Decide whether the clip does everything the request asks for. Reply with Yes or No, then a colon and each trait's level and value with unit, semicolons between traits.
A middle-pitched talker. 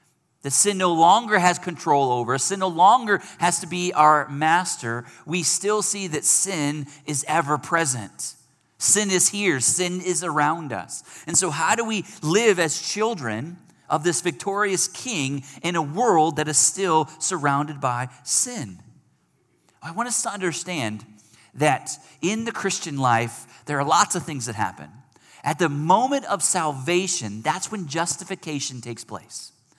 Yes: medium, 165 Hz